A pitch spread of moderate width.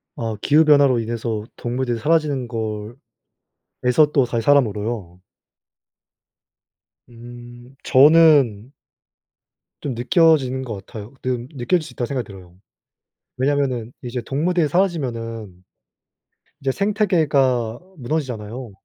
Yes: average, 4.0 semitones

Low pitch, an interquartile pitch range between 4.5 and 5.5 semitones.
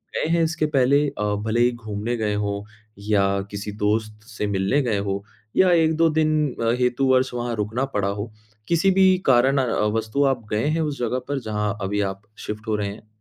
Yes: low, 115 Hz; average, 5.1 semitones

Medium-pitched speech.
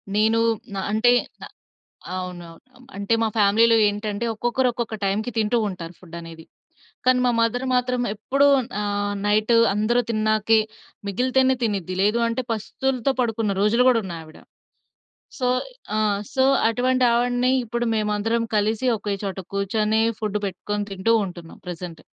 No: high, 215 Hz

